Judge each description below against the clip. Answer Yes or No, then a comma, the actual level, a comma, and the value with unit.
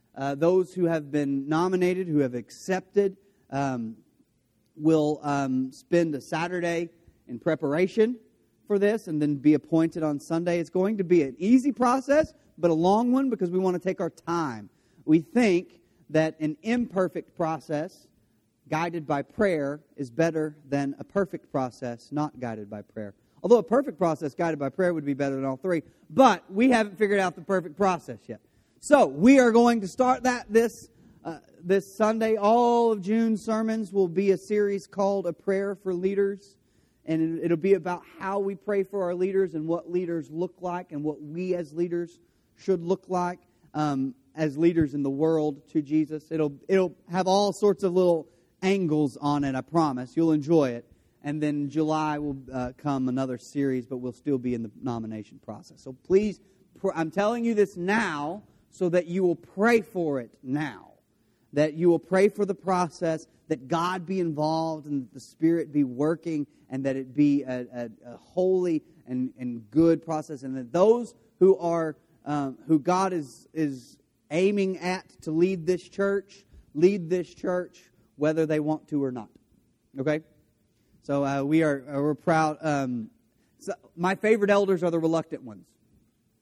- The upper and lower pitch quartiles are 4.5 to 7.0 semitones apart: Yes, average, 4.8 semitones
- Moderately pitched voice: Yes, medium, 165 Hz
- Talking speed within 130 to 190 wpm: Yes, average, 180 wpm